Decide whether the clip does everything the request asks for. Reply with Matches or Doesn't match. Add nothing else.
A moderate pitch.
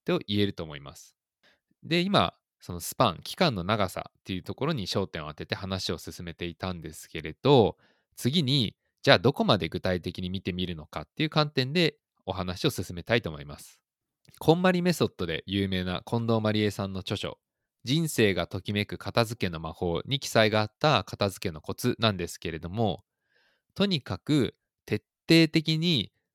Doesn't match